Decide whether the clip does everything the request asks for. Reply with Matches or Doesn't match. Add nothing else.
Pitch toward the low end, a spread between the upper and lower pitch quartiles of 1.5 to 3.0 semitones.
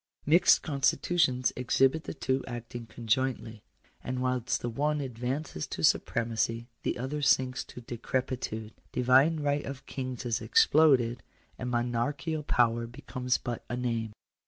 Matches